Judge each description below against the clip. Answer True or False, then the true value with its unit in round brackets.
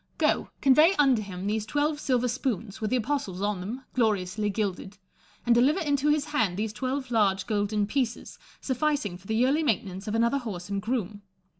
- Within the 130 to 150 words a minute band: False (180 wpm)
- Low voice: False (225 Hz)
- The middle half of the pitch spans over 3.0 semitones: True (4.7 semitones)